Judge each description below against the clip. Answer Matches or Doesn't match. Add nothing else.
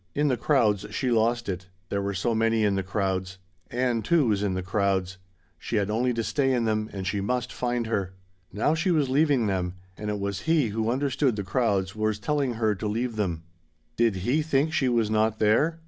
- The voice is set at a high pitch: Doesn't match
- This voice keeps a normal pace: Doesn't match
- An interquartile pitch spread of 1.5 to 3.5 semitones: Doesn't match